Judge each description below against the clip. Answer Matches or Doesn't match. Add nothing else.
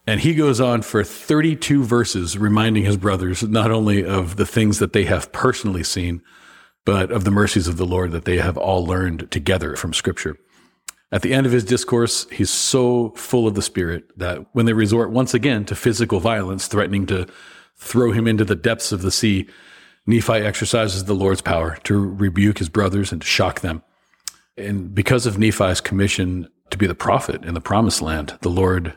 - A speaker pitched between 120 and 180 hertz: Doesn't match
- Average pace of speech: Matches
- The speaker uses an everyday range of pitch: Matches